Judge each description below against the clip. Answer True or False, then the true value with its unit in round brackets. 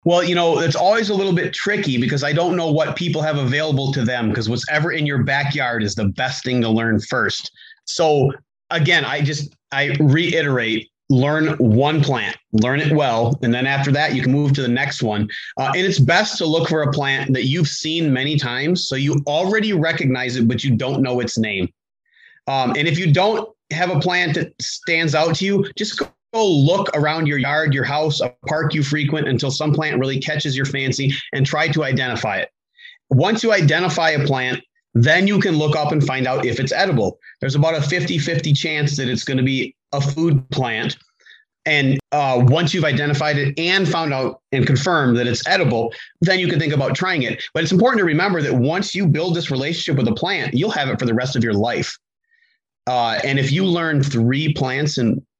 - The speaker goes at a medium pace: False (215 wpm)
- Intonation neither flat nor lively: True (4.0 semitones)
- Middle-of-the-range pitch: True (145 Hz)